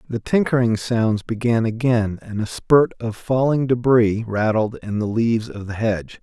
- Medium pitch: No, low, 115 Hz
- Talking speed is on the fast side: No, average, 175 wpm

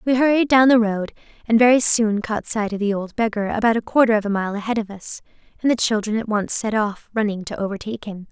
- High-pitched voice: Yes, high, 220 Hz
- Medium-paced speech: No, fast, 245 wpm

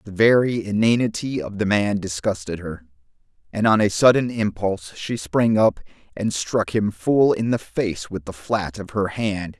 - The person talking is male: Yes, male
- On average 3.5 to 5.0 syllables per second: Yes, 4.5 syllables/s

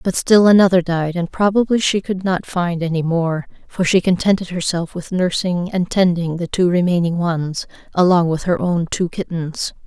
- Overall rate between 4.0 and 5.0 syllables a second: Yes, 4.8 syllables/s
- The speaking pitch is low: No, medium, 175 Hz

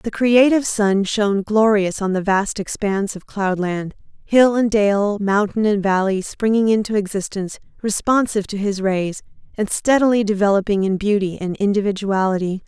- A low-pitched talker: No, high, 205 Hz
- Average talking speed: Yes, average, 145 wpm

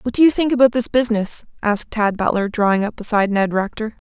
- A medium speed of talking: No, fast, 220 wpm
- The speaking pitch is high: Yes, high, 220 Hz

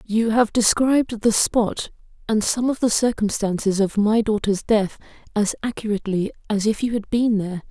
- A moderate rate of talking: Yes, average, 170 wpm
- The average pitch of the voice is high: Yes, high, 215 Hz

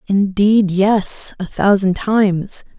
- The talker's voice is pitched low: No, high, 200 Hz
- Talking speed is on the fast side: No, slow, 110 wpm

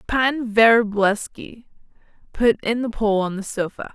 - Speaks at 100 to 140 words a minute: Yes, slow, 135 wpm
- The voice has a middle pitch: No, high, 220 Hz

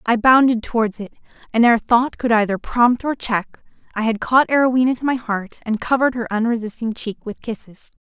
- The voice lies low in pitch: No, high, 235 Hz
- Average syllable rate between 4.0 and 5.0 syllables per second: No, 5.4 syllables/s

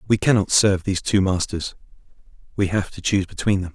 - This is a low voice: Yes, very low, 95 Hz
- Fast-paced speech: No, average, 190 wpm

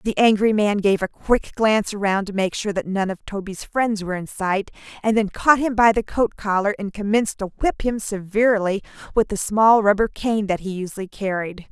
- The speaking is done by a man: No, female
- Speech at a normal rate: No, fast, 215 wpm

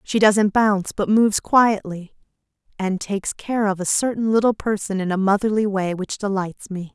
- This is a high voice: Yes, high, 205 Hz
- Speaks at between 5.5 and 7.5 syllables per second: No, 5.0 syllables/s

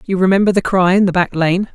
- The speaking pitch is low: No, medium, 185 Hz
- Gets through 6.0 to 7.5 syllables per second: Yes, 6.2 syllables/s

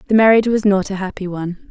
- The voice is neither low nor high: No, high, 200 Hz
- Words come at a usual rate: No, fast, 245 wpm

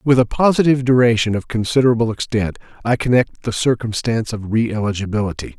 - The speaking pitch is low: Yes, low, 115 Hz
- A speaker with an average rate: Yes, average, 150 wpm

